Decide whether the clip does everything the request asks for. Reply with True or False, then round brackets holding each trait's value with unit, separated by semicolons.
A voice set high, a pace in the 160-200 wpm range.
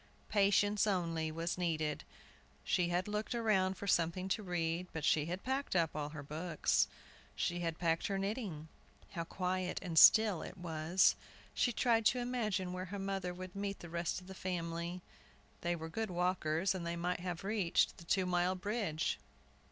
False (180 Hz; 175 wpm)